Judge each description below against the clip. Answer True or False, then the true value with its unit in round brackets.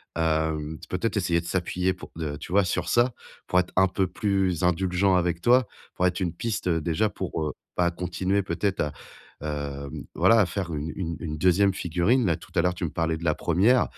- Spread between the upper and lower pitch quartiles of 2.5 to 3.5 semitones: True (2.8 semitones)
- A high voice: False (90 Hz)